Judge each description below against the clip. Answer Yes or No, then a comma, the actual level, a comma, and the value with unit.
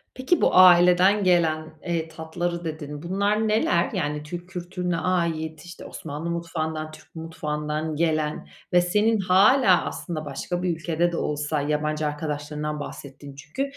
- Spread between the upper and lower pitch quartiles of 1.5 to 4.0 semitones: Yes, average, 2.8 semitones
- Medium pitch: Yes, medium, 165 Hz